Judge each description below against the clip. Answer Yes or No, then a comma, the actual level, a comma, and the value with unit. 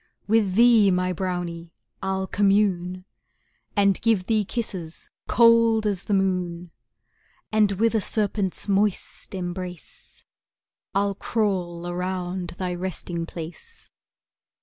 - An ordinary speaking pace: No, slow, 105 wpm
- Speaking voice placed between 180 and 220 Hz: Yes, high, 190 Hz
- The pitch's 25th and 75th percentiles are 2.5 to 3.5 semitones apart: Yes, average, 2.9 semitones